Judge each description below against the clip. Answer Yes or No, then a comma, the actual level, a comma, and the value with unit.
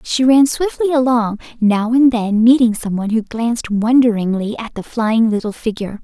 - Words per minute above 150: Yes, average, 170 wpm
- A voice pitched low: No, high, 230 Hz